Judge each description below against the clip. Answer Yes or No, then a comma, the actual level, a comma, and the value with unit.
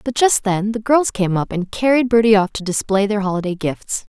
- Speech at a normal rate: No, fast, 230 wpm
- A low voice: No, high, 210 Hz